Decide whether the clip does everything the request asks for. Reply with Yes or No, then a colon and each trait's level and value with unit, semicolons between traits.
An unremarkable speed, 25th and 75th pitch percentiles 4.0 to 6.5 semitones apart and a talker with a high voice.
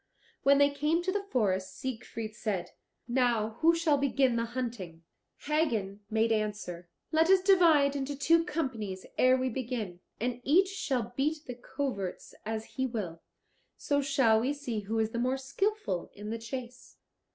Yes: average, 165 wpm; average, 4.6 semitones; very high, 250 Hz